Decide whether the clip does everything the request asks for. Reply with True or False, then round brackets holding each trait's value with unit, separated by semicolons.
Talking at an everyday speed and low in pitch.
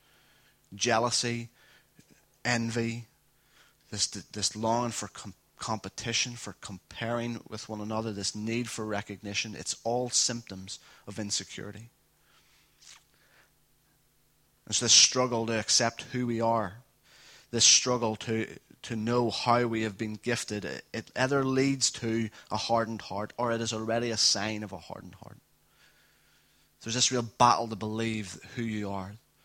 False (130 wpm; 115 Hz)